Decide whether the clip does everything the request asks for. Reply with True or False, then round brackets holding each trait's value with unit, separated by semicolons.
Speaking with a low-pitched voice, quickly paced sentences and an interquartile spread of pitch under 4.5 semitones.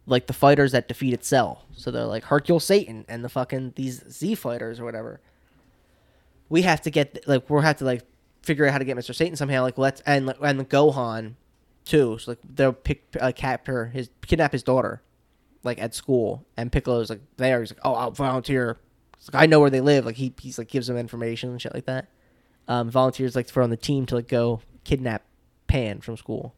True (130 Hz; 220 wpm; 2.9 semitones)